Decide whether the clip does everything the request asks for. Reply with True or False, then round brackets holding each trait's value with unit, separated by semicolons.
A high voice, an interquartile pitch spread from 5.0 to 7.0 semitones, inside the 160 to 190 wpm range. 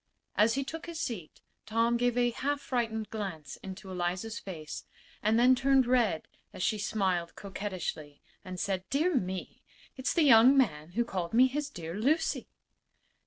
True (220 Hz; 5.6 semitones; 165 wpm)